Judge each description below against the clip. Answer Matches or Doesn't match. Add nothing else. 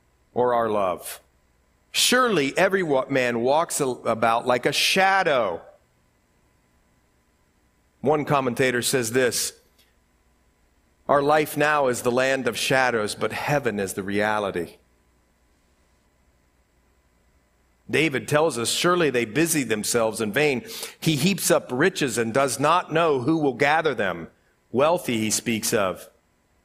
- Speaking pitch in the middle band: Doesn't match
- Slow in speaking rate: Matches